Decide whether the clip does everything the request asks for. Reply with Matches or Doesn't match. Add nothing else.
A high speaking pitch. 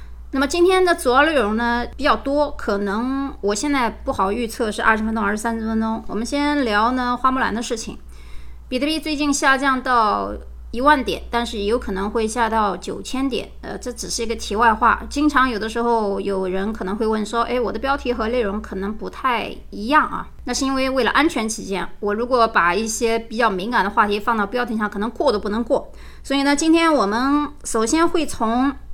Matches